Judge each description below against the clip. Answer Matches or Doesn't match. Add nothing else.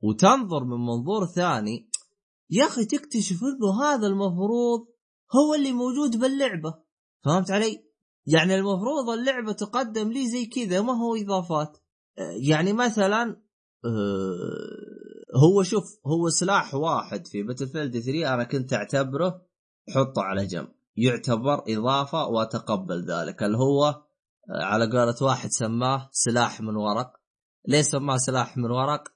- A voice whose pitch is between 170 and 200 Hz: Doesn't match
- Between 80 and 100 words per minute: Doesn't match